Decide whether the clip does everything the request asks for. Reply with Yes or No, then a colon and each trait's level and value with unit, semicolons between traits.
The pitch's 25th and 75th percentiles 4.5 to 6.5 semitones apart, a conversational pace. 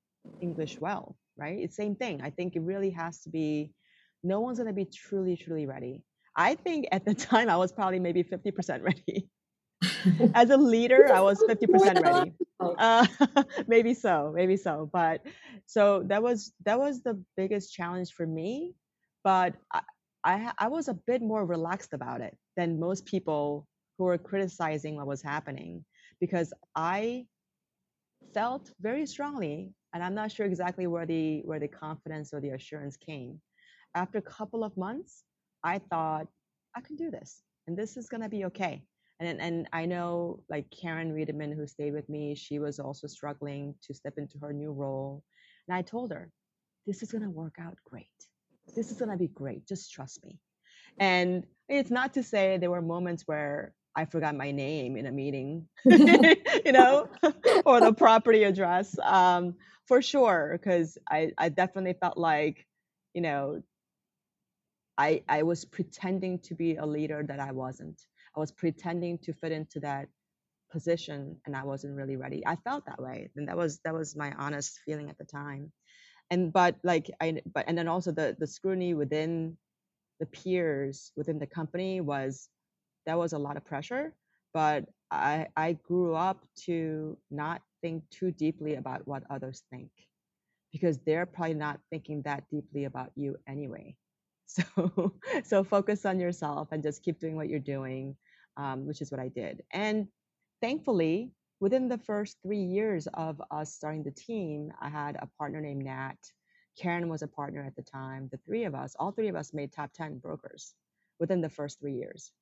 Yes: average, 4.9 semitones; average, 180 wpm